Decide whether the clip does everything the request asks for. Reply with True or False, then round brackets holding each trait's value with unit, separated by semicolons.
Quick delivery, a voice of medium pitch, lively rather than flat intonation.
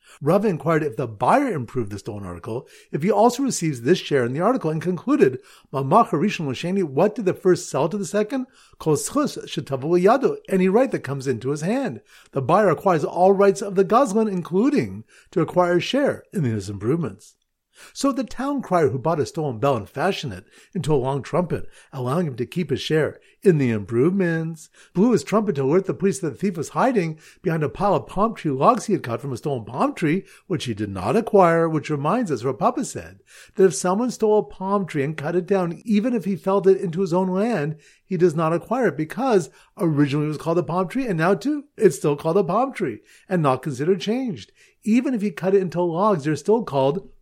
True (215 wpm; 180 Hz; 5.9 semitones)